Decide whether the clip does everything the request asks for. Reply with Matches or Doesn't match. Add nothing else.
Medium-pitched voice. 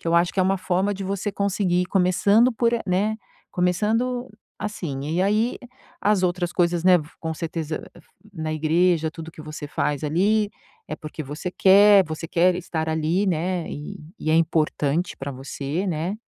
Matches